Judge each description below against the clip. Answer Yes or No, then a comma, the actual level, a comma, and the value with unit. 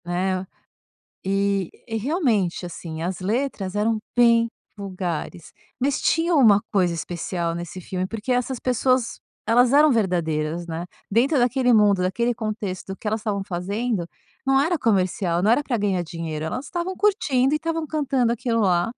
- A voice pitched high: Yes, high, 210 Hz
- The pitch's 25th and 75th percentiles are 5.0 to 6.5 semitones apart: Yes, wide, 5.5 semitones